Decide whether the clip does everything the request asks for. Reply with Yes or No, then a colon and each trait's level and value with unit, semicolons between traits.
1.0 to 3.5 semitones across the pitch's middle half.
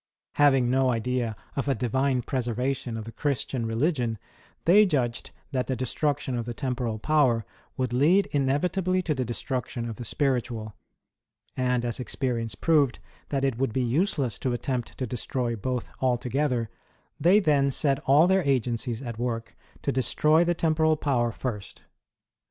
Yes: average, 3.2 semitones